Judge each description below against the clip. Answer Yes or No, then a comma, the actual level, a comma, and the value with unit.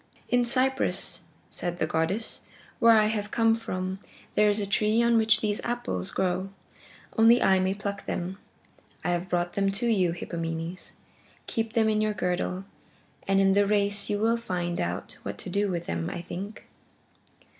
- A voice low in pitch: No, high, 200 Hz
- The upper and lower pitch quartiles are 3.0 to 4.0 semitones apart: Yes, average, 3.7 semitones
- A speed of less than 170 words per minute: No, average, 175 wpm